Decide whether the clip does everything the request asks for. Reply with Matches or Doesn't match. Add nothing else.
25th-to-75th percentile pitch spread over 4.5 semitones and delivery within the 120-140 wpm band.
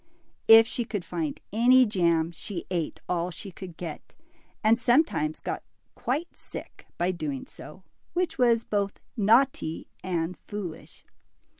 Matches